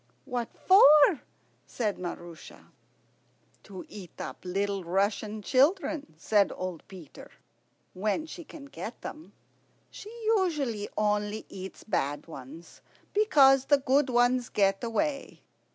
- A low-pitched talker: No, high, 220 Hz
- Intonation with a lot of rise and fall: Yes, wide, 6.6 semitones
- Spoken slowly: Yes, slow, 115 wpm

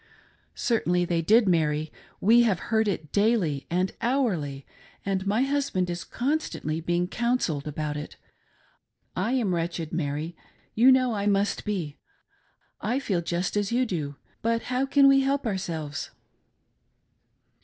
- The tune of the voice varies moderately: No, wide, 6.2 semitones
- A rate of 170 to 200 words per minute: No, average, 145 wpm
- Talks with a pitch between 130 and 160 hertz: No, high, 195 Hz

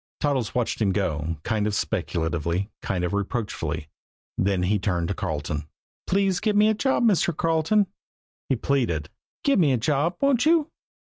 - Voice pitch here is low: Yes, low, 115 Hz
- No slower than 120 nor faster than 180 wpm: Yes, average, 165 wpm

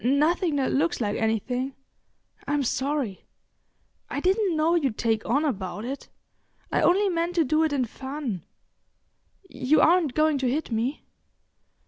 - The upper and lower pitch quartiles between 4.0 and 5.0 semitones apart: Yes, average, 4.3 semitones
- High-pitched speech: Yes, very high, 280 Hz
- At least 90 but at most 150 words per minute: Yes, average, 140 wpm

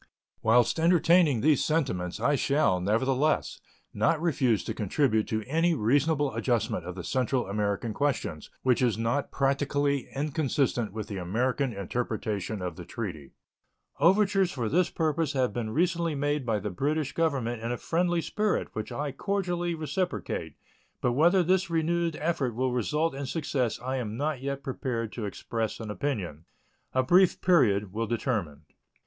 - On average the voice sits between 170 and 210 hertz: No, low, 130 Hz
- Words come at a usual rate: Yes, average, 155 wpm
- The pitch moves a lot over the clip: Yes, wide, 6.0 semitones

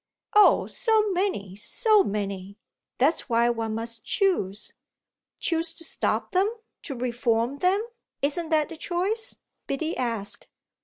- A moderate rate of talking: No, slow, 125 wpm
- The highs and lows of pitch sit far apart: Yes, wide, 8.3 semitones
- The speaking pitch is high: Yes, very high, 280 Hz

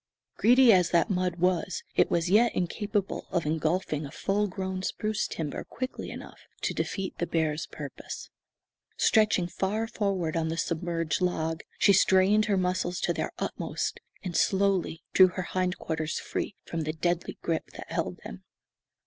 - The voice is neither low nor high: Yes, medium, 180 Hz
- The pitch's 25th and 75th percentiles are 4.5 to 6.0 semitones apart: No, average, 3.1 semitones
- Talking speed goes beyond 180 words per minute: No, average, 160 wpm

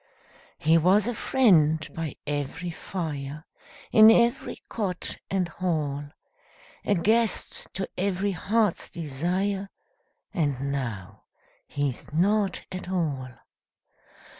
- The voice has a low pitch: No, medium, 175 Hz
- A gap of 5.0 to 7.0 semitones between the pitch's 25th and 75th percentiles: Yes, average, 5.3 semitones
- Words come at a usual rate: No, slow, 100 wpm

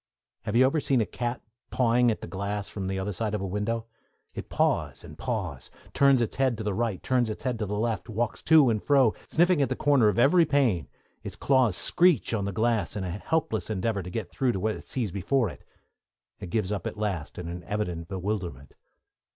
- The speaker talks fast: Yes, fast, 225 wpm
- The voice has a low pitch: Yes, low, 110 Hz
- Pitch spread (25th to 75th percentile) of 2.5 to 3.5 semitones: No, average, 4.3 semitones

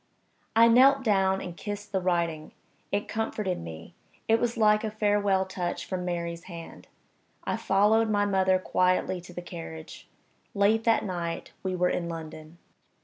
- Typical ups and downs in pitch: Yes, average, 3.5 semitones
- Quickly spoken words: No, average, 155 wpm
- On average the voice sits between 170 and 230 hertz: Yes, high, 190 Hz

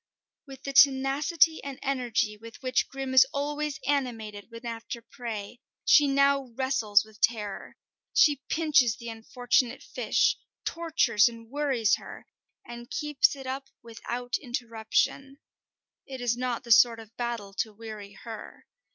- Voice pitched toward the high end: Yes, high, 245 Hz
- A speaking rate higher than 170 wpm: No, average, 140 wpm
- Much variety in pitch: No, average, 3.3 semitones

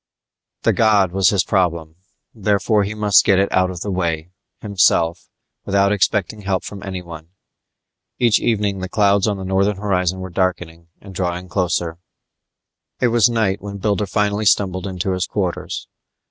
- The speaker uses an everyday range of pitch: No, narrow, 2.2 semitones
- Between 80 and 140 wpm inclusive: No, average, 160 wpm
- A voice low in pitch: Yes, very low, 95 Hz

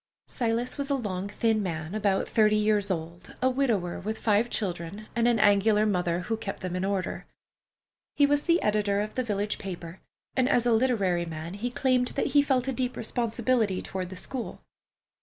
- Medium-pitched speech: No, high, 210 Hz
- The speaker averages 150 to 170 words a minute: No, average, 190 wpm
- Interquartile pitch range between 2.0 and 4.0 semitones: No, average, 4.4 semitones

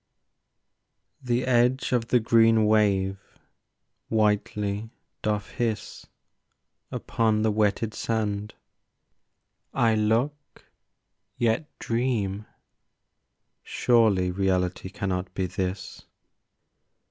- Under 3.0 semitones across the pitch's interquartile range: Yes, narrow, 2.6 semitones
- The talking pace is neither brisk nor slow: No, slow, 75 wpm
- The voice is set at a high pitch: No, low, 110 Hz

